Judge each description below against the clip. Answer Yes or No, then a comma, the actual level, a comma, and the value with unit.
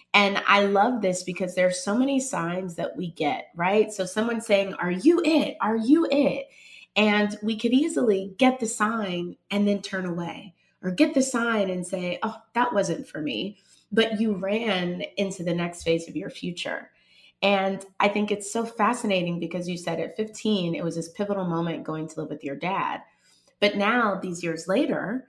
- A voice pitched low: No, high, 200 Hz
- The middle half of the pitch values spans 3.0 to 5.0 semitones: Yes, average, 3.8 semitones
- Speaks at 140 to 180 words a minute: No, average, 195 wpm